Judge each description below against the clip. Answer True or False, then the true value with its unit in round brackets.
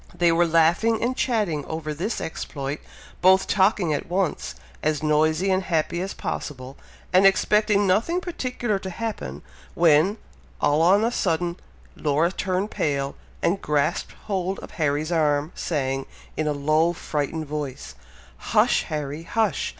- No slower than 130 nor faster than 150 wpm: True (140 wpm)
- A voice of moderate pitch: True (165 Hz)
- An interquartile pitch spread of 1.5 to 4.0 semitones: False (4.4 semitones)